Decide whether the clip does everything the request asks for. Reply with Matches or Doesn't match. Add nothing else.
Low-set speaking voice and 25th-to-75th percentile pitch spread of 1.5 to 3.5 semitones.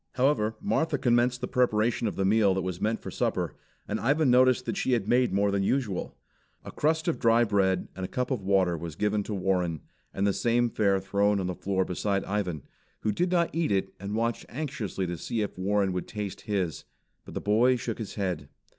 Doesn't match